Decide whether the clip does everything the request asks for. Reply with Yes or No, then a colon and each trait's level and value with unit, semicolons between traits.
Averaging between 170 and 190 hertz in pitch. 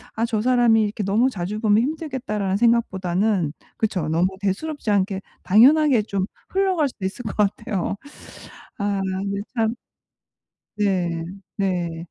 No: high, 210 Hz